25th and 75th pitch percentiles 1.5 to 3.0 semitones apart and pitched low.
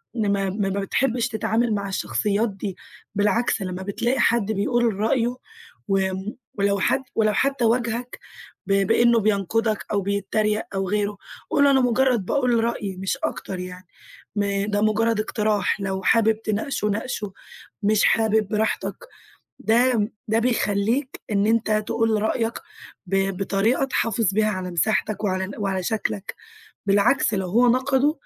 No: average, 2.7 semitones; high, 215 Hz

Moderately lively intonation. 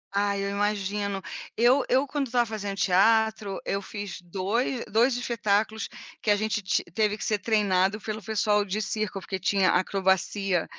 No: narrow, 2.1 semitones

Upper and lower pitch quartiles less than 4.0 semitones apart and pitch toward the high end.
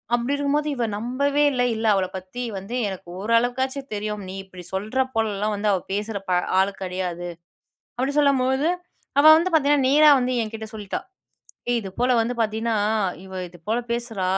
No: average, 4.8 semitones; high, 225 Hz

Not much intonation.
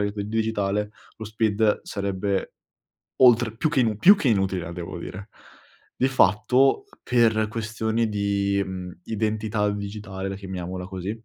Yes: narrow, 2.3 semitones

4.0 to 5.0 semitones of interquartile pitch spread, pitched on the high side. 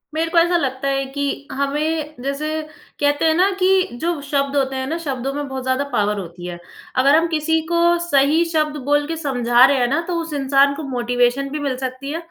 No: average, 2.9 semitones; very high, 280 Hz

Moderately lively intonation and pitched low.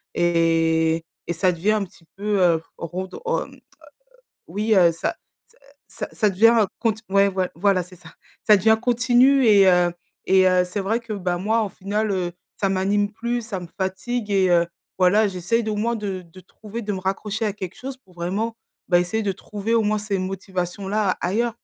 No: average, 3.1 semitones; high, 195 Hz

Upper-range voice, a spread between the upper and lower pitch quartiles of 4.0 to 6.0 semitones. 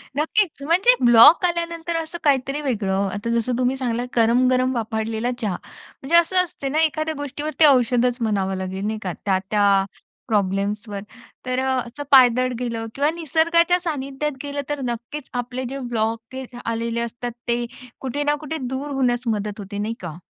Yes: very high, 250 Hz; average, 4.5 semitones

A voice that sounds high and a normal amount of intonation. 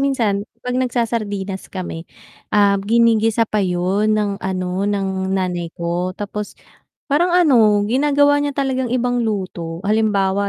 Yes: high, 210 Hz; average, 4.0 semitones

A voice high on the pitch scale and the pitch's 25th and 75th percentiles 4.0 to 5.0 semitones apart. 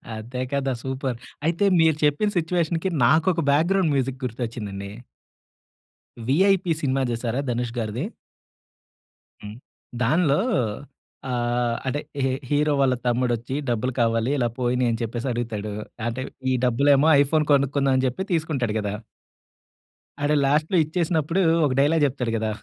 No: low, 130 Hz; average, 4.3 semitones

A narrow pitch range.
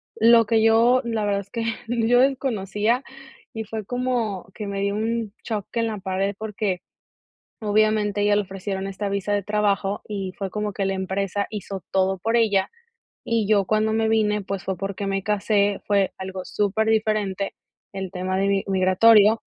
Yes: narrow, 2.1 semitones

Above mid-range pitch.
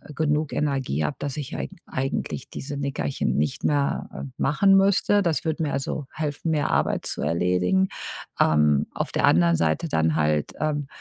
No: medium, 140 Hz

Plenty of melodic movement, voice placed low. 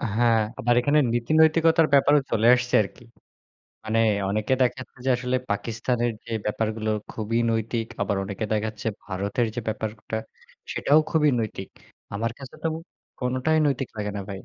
No: average, 3.3 semitones; low, 115 Hz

